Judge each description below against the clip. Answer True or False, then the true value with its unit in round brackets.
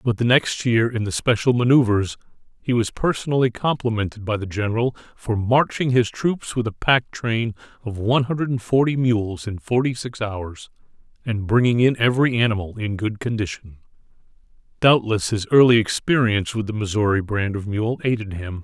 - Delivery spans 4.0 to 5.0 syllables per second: False (5.2 syllables/s)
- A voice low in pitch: True (115 Hz)